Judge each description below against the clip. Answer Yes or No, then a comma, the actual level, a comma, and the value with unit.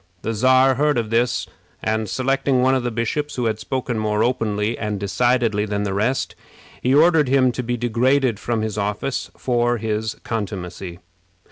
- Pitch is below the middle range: Yes, low, 115 Hz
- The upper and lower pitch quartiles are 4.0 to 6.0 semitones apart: No, average, 3.3 semitones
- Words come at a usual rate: Yes, average, 170 wpm